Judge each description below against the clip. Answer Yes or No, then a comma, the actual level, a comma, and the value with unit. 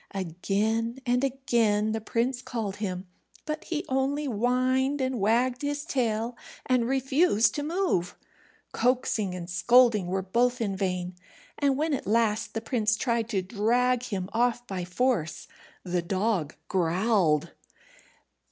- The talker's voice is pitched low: No, high, 230 Hz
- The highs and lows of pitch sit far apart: No, average, 4.7 semitones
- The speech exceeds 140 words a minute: No, slow, 135 wpm